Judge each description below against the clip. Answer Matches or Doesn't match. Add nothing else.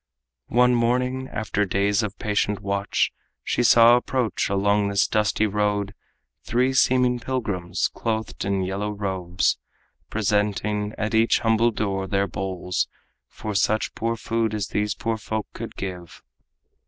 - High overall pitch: Doesn't match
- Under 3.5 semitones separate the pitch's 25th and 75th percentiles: Matches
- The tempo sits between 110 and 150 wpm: Matches